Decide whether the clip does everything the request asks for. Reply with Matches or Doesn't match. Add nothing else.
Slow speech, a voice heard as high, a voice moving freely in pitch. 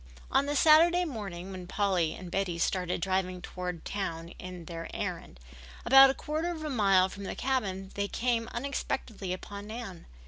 Doesn't match